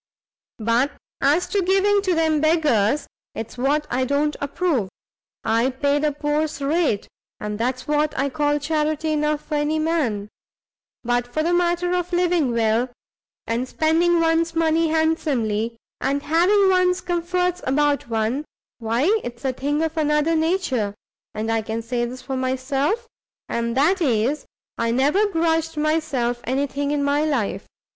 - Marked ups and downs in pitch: No, average, 4.7 semitones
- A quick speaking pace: No, average, 150 wpm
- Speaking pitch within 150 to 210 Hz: No, very high, 295 Hz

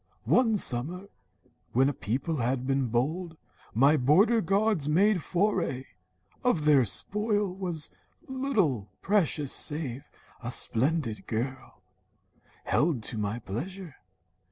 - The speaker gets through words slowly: Yes, slow, 110 wpm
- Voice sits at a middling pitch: Yes, medium, 150 Hz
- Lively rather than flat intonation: Yes, wide, 7.3 semitones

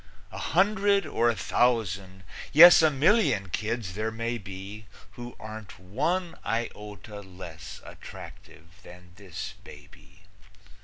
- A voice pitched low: Yes, low, 110 Hz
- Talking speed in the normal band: No, slow, 115 wpm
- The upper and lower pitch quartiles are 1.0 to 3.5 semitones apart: No, average, 4.6 semitones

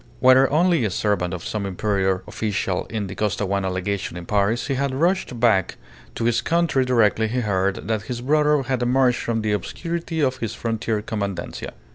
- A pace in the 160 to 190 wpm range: Yes, average, 180 wpm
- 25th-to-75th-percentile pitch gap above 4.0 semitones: Yes, average, 4.6 semitones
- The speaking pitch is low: Yes, low, 110 Hz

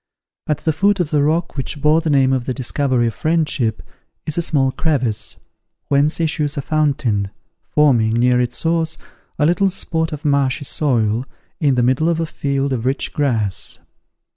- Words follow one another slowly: No, average, 175 wpm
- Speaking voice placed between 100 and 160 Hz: Yes, medium, 140 Hz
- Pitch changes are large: No, average, 3.9 semitones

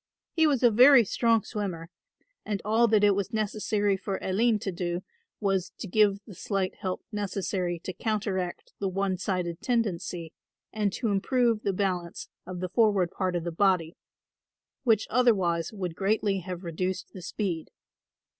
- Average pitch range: Yes, average, 3.0 semitones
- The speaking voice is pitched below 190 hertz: No, high, 195 Hz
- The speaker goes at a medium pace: Yes, average, 160 wpm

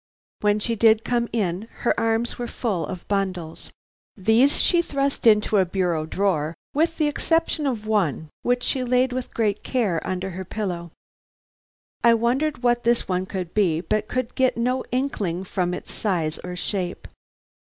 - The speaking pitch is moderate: No, high, 215 Hz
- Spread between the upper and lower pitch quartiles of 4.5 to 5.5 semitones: Yes, average, 5.2 semitones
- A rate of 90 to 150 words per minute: No, average, 165 wpm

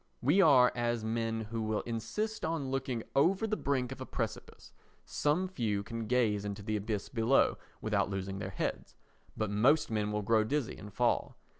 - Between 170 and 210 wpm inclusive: Yes, average, 180 wpm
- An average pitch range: Yes, average, 4.2 semitones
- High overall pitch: No, low, 115 Hz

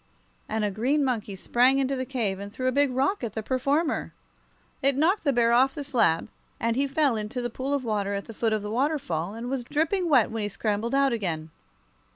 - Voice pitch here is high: Yes, high, 245 Hz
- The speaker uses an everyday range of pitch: Yes, average, 4.4 semitones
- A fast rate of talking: Yes, fast, 225 wpm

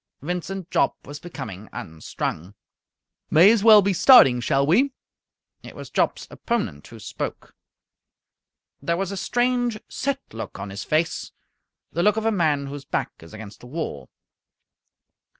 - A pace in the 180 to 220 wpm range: No, average, 150 wpm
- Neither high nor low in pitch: Yes, medium, 160 Hz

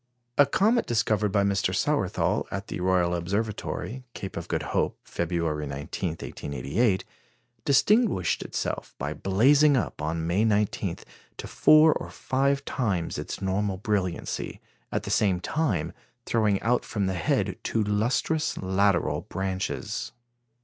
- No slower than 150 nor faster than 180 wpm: No, slow, 135 wpm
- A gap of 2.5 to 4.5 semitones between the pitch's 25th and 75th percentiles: No, average, 5.2 semitones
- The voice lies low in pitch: Yes, low, 100 Hz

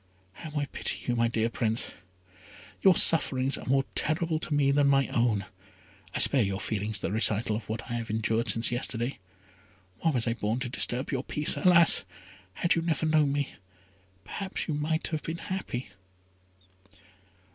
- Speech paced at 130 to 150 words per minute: No, average, 170 wpm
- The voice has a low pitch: Yes, low, 130 Hz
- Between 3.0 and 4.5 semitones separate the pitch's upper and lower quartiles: No, average, 5.3 semitones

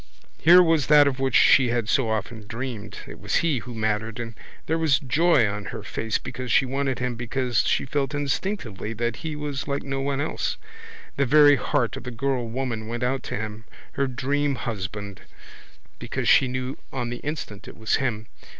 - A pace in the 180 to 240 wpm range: Yes, average, 185 wpm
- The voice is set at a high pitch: No, low, 125 Hz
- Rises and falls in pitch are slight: No, average, 3.7 semitones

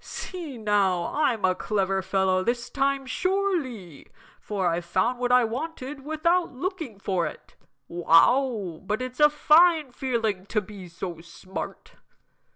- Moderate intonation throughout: No, wide, 6.8 semitones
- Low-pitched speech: No, high, 230 Hz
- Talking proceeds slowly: No, average, 145 wpm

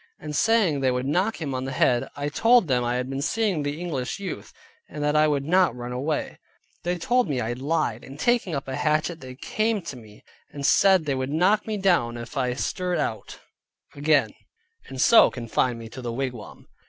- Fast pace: Yes, fast, 210 wpm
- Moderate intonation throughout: No, wide, 5.7 semitones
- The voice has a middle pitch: Yes, medium, 145 Hz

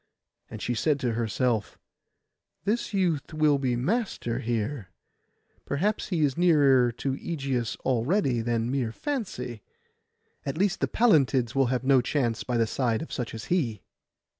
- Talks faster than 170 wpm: No, average, 150 wpm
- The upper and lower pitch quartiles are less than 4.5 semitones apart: No, average, 4.8 semitones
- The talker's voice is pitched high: No, low, 130 Hz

